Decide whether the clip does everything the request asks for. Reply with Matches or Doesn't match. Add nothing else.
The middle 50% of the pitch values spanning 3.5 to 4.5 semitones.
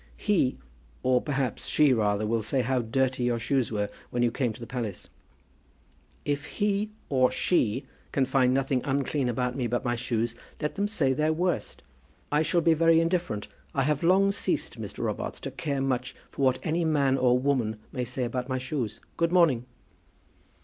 Matches